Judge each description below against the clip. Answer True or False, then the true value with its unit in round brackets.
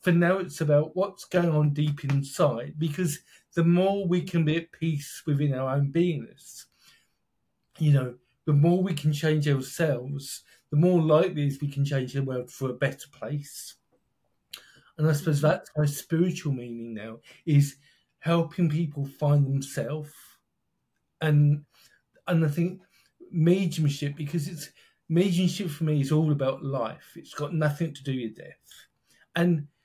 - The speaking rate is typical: True (155 wpm)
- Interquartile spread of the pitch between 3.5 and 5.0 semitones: False (3.0 semitones)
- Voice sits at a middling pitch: True (150 Hz)